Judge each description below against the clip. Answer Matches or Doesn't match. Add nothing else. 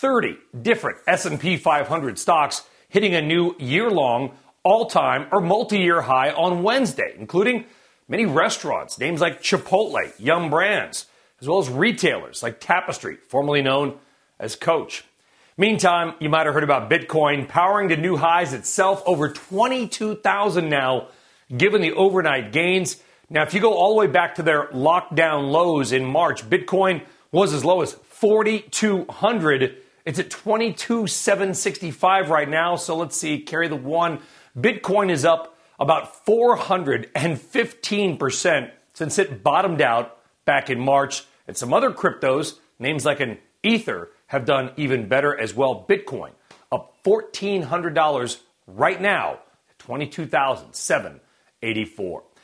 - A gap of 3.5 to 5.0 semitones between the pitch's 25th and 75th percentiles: Doesn't match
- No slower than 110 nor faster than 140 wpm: Matches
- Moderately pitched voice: Matches